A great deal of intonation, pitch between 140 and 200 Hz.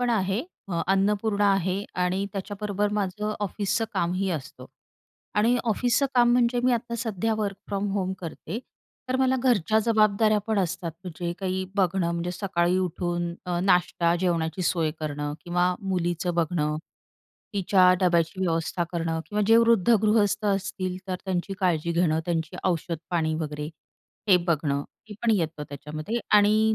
No: average, 3.5 semitones; medium, 185 Hz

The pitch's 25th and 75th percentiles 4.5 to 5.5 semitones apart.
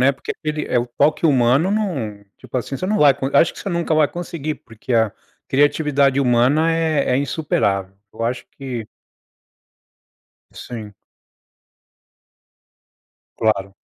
Yes: average, 4.8 semitones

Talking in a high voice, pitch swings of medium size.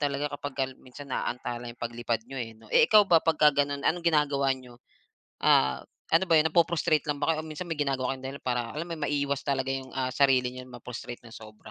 No: medium, 140 Hz; average, 3.2 semitones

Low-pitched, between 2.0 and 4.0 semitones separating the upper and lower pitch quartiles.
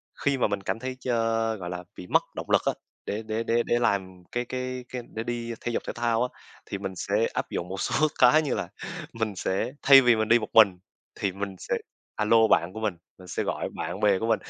Yes: low, 110 Hz; average, 3.5 semitones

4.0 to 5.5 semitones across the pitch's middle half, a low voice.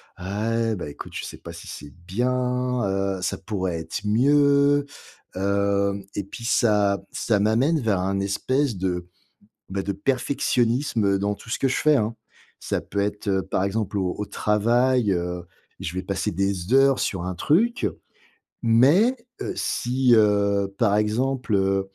Yes: average, 4.4 semitones; low, 105 Hz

